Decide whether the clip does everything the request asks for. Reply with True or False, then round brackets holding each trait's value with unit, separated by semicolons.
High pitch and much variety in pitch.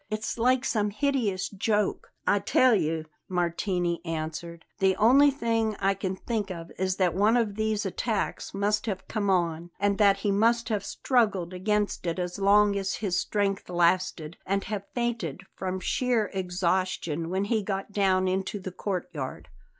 False (195 Hz; 2.9 semitones)